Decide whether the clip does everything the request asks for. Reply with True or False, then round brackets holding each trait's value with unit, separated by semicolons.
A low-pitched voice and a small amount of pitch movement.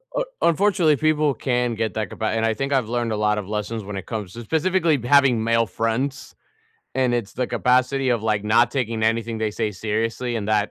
False (115 Hz; 3.5 semitones)